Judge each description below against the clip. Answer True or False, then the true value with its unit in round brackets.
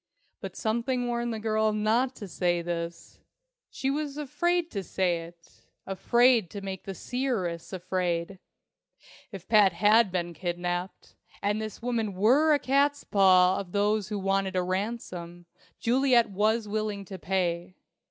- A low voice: False (205 Hz)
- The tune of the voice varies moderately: True (4.5 semitones)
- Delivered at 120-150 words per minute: True (145 wpm)